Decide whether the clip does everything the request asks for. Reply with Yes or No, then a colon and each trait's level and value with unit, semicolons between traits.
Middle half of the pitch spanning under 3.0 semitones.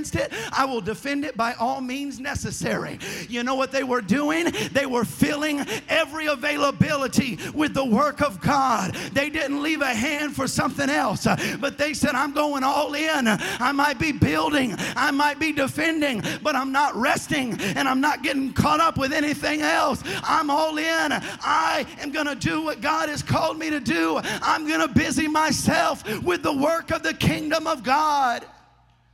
Yes: narrow, 2.5 semitones